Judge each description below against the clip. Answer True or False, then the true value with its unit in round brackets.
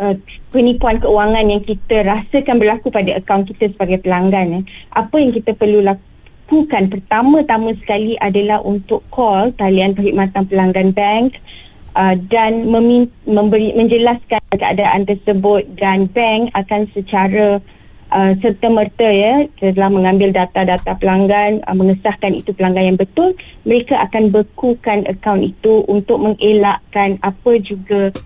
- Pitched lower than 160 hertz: False (210 Hz)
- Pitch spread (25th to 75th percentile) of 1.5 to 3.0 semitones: True (2.5 semitones)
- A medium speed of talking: True (130 wpm)